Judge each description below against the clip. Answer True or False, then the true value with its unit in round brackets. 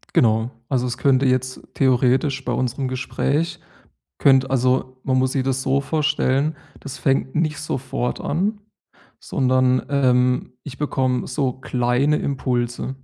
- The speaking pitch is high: False (130 Hz)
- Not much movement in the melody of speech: True (1.5 semitones)